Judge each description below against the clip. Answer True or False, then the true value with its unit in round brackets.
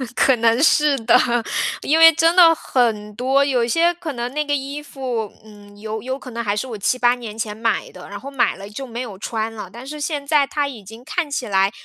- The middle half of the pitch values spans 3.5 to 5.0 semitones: True (4.6 semitones)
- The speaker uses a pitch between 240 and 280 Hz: True (245 Hz)